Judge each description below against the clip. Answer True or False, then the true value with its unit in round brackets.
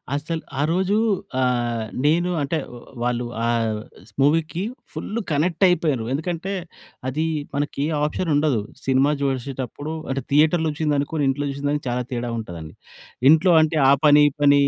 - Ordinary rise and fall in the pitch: True (3.2 semitones)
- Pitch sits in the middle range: True (145 Hz)